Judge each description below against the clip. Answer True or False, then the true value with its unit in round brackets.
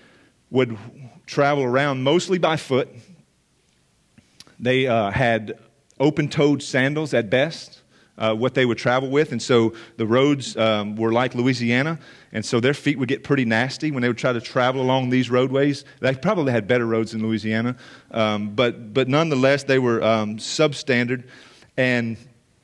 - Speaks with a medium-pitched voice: False (130 Hz)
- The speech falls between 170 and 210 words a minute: False (160 wpm)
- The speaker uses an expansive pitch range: False (3.1 semitones)